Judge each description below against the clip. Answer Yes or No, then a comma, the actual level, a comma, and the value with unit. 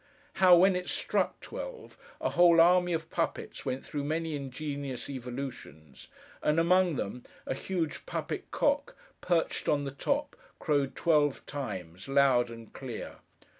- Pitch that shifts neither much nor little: Yes, average, 4.7 semitones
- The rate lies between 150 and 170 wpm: No, average, 140 wpm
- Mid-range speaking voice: Yes, medium, 145 Hz